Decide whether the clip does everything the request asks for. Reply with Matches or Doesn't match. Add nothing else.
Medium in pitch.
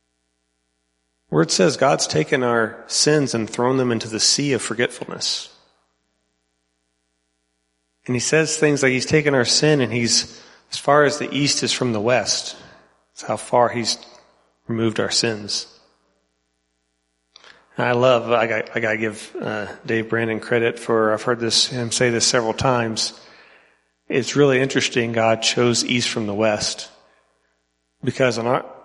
Doesn't match